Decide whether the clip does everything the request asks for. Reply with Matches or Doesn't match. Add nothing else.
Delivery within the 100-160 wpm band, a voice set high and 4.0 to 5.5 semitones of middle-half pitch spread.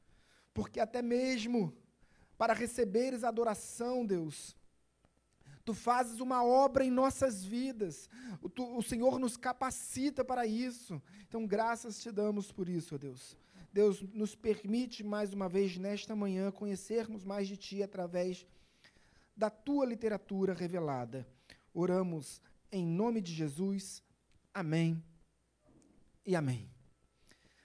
Matches